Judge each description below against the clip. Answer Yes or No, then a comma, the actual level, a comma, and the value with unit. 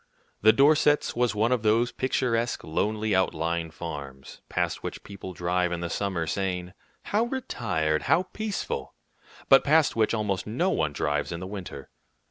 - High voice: No, low, 100 Hz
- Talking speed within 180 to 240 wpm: No, average, 155 wpm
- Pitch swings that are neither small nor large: No, wide, 6.3 semitones